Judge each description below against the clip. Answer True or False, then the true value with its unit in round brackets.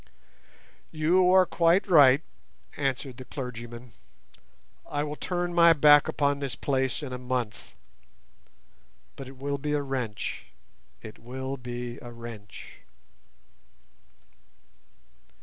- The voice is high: False (135 Hz)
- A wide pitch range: False (3.4 semitones)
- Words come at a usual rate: False (115 wpm)